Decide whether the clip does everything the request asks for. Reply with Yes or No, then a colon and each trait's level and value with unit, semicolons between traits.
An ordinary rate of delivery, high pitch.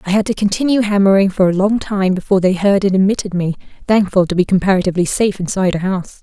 No: fast, 220 wpm; high, 195 Hz